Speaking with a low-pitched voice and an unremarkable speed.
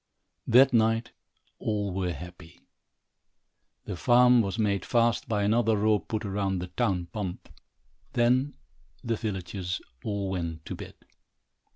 No: low, 105 Hz; slow, 130 wpm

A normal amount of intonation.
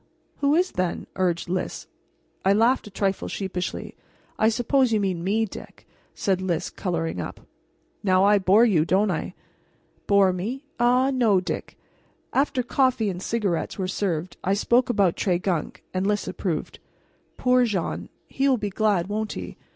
Yes: average, 4.1 semitones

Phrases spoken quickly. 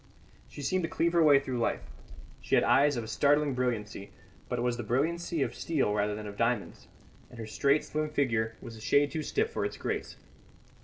Yes: fast, 210 wpm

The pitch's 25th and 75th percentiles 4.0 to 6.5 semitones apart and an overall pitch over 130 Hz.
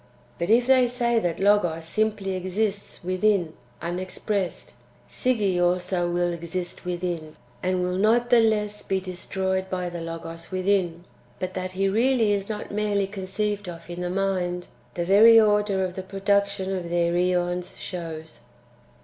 No: average, 2.7 semitones; medium, 185 Hz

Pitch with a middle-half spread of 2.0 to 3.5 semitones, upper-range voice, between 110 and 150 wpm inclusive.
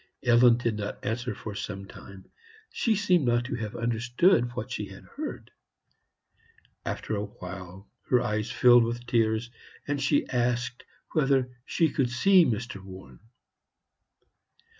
No: average, 2.9 semitones; low, 120 Hz; average, 140 wpm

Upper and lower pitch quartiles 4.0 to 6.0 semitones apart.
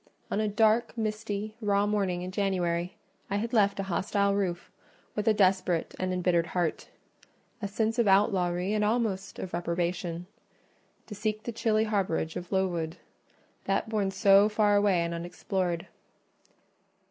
No: average, 3.1 semitones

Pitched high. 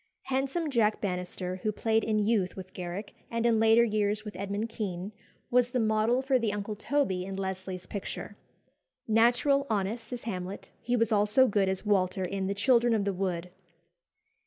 Yes: high, 210 Hz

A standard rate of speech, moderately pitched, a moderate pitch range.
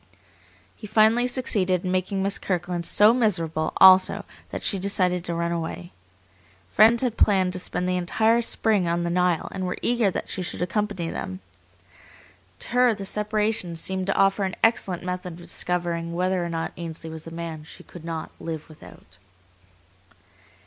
Yes: average, 170 wpm; medium, 180 Hz; average, 3.5 semitones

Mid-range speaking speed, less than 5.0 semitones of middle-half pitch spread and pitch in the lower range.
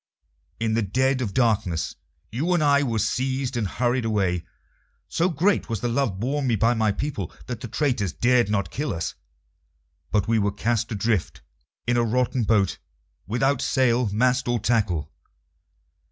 Yes: average, 165 wpm; average, 3.7 semitones; low, 115 Hz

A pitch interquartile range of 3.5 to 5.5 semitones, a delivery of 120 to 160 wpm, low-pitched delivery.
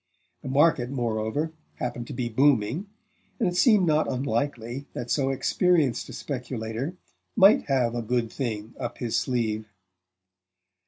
Yes: average, 3.9 semitones; average, 140 wpm; low, 125 Hz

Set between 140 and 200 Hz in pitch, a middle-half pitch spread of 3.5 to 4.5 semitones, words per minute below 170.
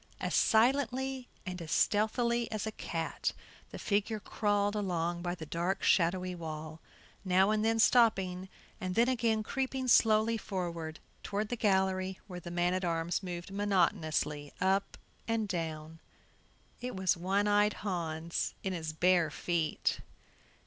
Yes: high, 190 Hz; average, 3.9 semitones; average, 140 wpm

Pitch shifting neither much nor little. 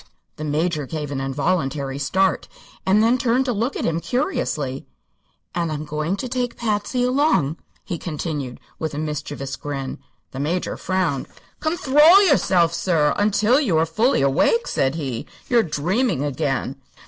No: wide, 8.0 semitones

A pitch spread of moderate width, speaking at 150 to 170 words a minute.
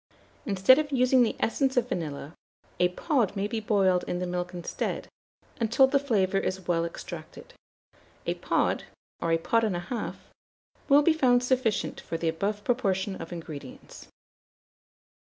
No: wide, 6.1 semitones; average, 155 wpm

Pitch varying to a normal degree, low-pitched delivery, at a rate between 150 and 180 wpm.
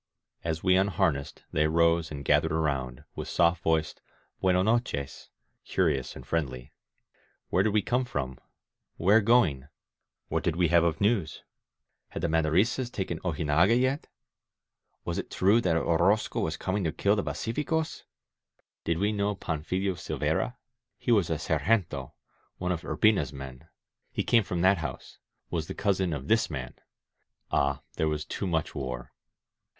Yes: average, 4.7 semitones; very low, 85 Hz; average, 155 wpm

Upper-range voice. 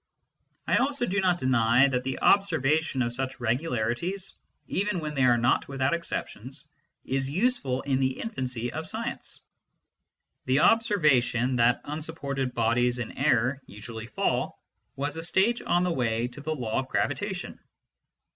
No: low, 135 Hz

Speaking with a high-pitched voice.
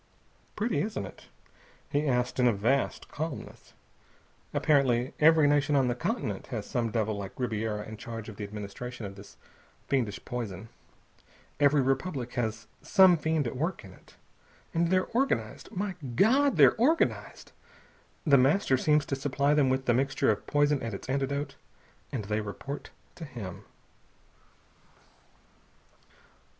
No: low, 130 Hz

